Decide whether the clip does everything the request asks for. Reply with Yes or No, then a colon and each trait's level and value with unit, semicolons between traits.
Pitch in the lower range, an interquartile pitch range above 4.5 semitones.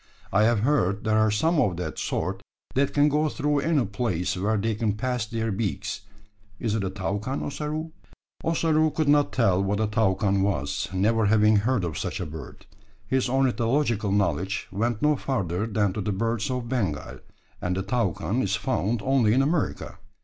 Yes: low, 110 Hz; average, 5.0 semitones